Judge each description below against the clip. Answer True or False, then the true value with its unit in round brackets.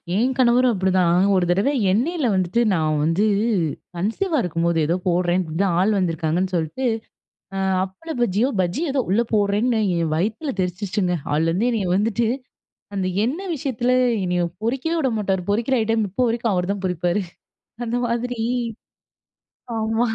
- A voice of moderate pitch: False (205 Hz)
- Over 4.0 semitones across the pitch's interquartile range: True (5.1 semitones)